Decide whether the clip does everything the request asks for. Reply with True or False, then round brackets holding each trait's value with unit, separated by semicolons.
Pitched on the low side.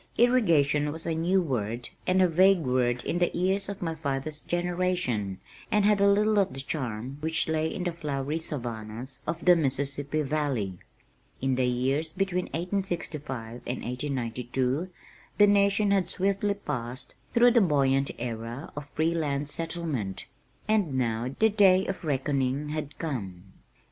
False (150 Hz)